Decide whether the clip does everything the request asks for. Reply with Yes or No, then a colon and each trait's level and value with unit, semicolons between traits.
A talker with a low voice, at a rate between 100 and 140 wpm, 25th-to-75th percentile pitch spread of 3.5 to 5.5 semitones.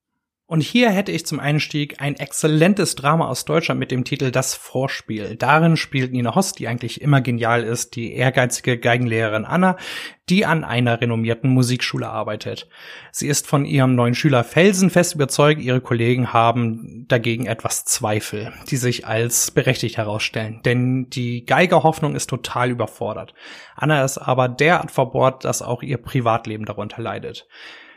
No: low, 125 Hz; average, 150 wpm; average, 4.0 semitones